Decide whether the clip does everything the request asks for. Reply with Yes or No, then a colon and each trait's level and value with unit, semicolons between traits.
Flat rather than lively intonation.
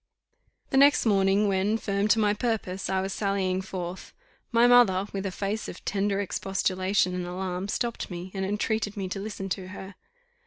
Yes: narrow, 1.8 semitones